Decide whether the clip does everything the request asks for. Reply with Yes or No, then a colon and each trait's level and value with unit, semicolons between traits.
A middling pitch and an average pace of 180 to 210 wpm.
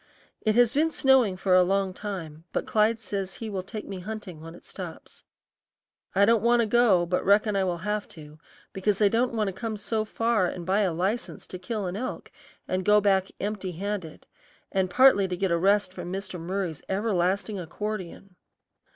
No: high, 195 Hz; average, 195 wpm